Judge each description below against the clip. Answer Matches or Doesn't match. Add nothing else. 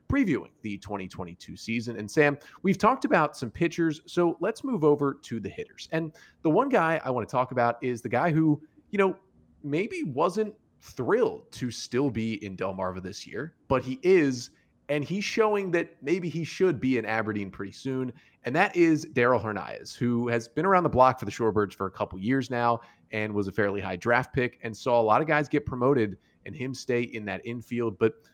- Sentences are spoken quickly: Matches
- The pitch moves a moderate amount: Doesn't match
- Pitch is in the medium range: Doesn't match